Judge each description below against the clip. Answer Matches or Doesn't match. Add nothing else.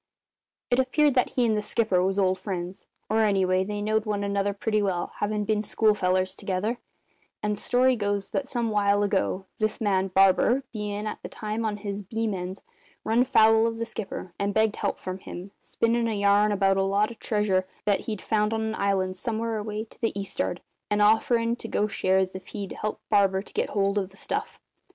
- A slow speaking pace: Doesn't match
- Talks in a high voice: Matches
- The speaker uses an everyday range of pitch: Doesn't match